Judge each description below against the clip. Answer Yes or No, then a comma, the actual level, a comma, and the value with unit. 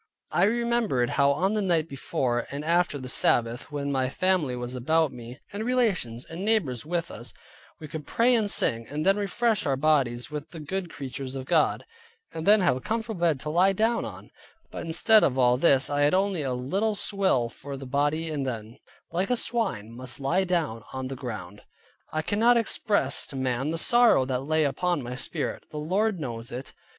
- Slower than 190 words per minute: No, average, 200 wpm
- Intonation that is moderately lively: No, wide, 6.8 semitones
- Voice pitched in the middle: Yes, medium, 150 Hz